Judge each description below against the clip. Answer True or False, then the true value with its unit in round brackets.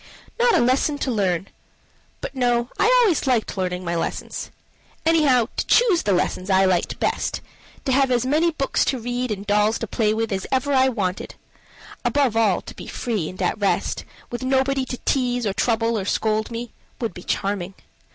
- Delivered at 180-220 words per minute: True (190 wpm)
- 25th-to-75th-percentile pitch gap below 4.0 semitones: False (4.7 semitones)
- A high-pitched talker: True (235 Hz)